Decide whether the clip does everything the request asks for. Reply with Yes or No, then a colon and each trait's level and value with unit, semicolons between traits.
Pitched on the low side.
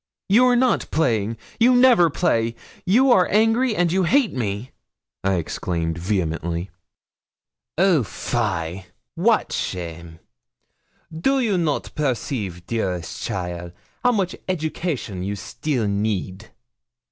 Yes: low, 120 Hz